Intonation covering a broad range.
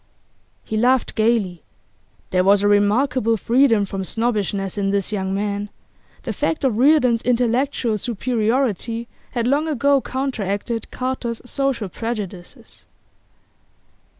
No: average, 3.8 semitones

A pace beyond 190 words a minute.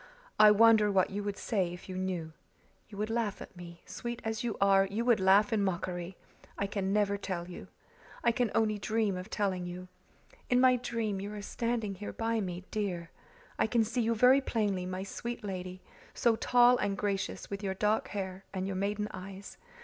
Yes: average, 200 wpm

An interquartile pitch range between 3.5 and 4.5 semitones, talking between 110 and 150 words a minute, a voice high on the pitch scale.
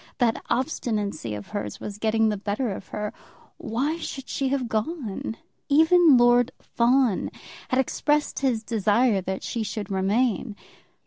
Yes: average, 4.2 semitones; average, 140 wpm; high, 230 Hz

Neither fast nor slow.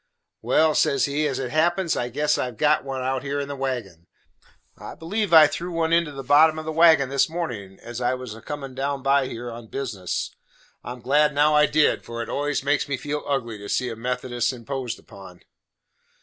No: fast, 220 wpm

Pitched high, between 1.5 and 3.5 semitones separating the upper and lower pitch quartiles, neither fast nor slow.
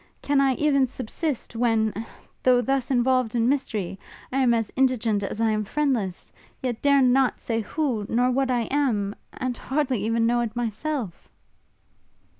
Yes: high, 245 Hz; average, 3.2 semitones; average, 160 wpm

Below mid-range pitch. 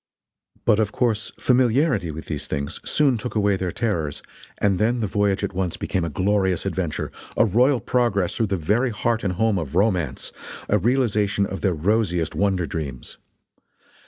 Yes: low, 100 Hz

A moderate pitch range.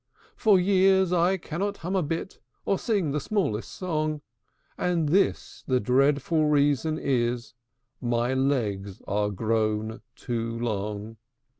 No: wide, 7.5 semitones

